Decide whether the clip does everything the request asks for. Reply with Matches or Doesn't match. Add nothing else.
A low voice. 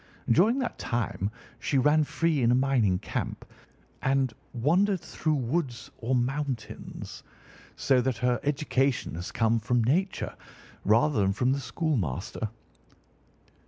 Matches